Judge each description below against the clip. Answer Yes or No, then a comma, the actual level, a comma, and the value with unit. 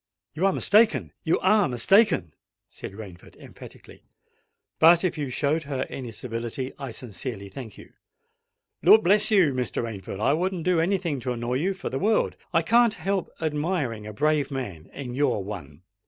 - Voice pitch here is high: No, medium, 140 Hz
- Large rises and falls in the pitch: Yes, wide, 7.6 semitones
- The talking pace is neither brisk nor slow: Yes, average, 160 wpm